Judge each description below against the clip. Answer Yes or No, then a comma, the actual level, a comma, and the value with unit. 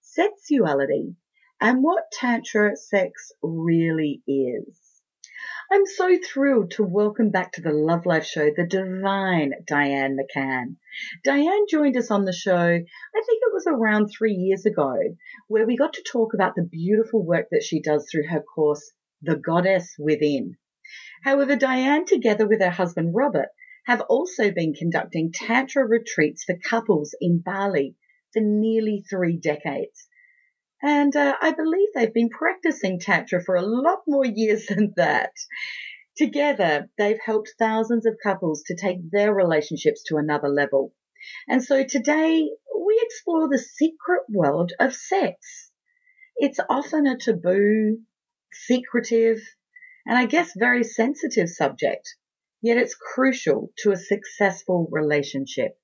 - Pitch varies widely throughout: Yes, wide, 8.5 semitones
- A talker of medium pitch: No, high, 220 Hz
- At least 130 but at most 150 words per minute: Yes, average, 140 wpm